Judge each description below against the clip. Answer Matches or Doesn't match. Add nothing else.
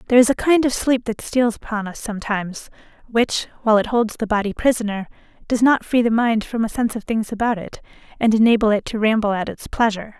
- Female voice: Matches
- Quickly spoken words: Matches